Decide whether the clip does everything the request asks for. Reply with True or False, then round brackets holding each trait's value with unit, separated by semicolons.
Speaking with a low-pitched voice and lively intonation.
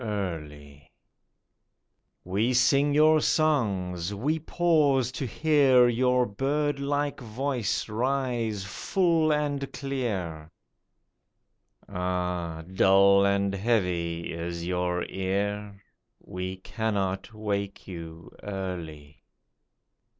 True (100 Hz; 6.8 semitones)